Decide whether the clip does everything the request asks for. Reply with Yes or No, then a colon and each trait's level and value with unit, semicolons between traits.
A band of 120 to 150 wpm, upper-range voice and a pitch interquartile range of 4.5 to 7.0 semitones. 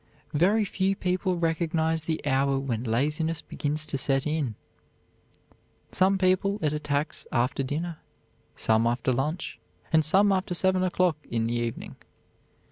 No: slow, 135 wpm; medium, 155 Hz; average, 5.1 semitones